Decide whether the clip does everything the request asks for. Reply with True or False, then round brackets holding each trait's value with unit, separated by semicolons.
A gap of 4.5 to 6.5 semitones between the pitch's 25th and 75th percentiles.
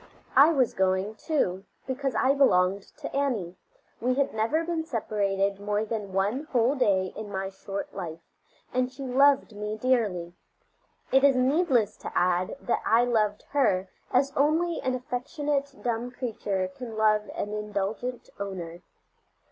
True (5.2 semitones)